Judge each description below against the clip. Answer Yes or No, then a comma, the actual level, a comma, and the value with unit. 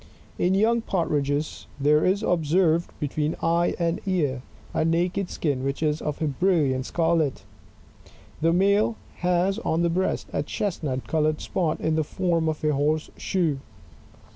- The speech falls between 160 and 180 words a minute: No, average, 150 wpm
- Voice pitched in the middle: Yes, medium, 165 Hz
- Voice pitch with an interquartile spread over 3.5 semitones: No, average, 3.0 semitones